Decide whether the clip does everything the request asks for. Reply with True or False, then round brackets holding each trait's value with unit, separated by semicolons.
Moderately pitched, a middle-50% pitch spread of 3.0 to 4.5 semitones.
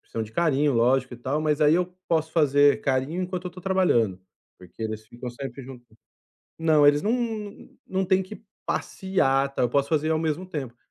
False (150 Hz; 5.6 semitones)